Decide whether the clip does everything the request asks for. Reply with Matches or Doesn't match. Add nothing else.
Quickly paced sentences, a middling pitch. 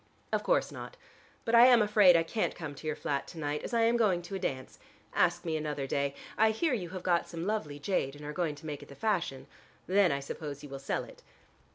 Matches